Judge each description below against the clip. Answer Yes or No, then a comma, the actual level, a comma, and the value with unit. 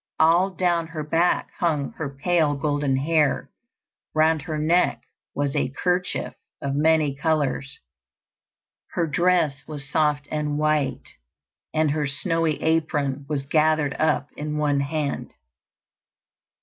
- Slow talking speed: Yes, slow, 125 wpm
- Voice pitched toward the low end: No, medium, 150 Hz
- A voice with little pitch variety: Yes, narrow, 2.1 semitones